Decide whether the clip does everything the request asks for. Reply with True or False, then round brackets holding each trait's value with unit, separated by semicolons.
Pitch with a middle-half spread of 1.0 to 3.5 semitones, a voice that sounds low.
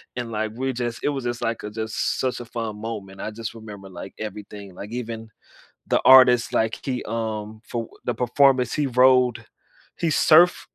True (2.6 semitones; 115 Hz)